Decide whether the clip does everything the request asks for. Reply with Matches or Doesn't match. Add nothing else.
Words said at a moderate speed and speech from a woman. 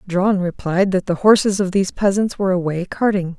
Matches